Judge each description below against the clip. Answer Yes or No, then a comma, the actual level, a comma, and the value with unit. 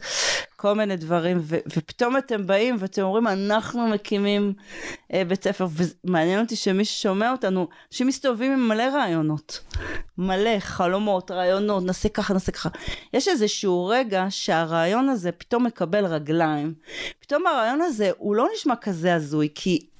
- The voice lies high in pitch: Yes, high, 195 Hz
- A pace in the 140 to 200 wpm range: Yes, average, 145 wpm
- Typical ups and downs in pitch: Yes, average, 3.9 semitones